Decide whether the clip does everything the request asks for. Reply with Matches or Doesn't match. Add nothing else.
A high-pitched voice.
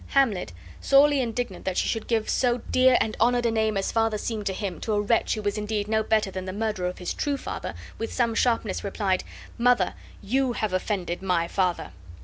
Matches